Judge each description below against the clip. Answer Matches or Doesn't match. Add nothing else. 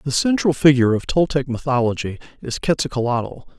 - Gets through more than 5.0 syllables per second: Matches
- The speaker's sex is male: Matches